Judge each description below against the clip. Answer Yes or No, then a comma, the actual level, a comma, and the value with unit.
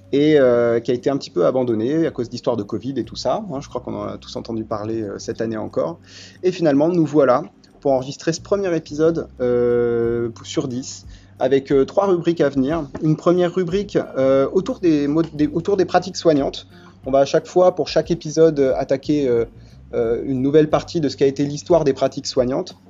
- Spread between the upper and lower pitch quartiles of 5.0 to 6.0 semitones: Yes, wide, 5.5 semitones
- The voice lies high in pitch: No, medium, 140 Hz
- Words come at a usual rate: Yes, average, 210 wpm